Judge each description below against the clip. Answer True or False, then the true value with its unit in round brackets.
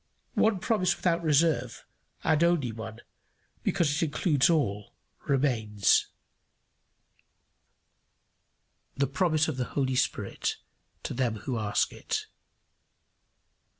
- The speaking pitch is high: False (140 Hz)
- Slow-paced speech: True (100 wpm)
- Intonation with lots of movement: True (6.1 semitones)